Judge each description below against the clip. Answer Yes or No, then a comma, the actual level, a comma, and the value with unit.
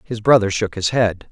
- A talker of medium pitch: No, low, 105 Hz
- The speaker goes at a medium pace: No, fast, 230 wpm